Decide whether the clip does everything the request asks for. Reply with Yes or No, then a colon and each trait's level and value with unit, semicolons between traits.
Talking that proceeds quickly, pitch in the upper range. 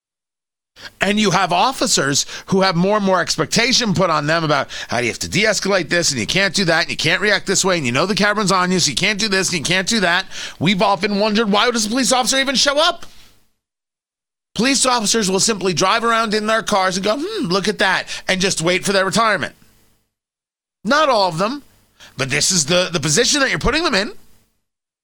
Yes: fast, 230 wpm; high, 195 Hz